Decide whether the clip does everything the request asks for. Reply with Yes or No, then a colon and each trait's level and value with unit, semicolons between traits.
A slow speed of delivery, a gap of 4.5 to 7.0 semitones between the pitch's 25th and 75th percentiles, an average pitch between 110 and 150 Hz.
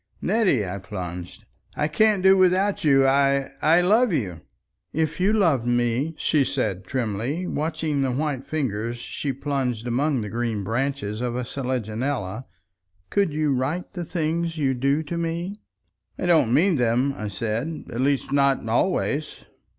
No: average, 150 wpm; average, 5.2 semitones; medium, 140 Hz